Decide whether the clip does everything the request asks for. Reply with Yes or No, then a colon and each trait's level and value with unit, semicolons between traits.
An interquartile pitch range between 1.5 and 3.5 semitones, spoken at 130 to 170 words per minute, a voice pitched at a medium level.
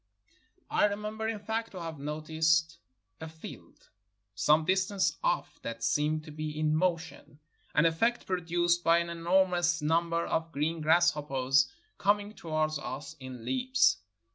Yes: average, 3.2 semitones; average, 140 wpm; medium, 165 Hz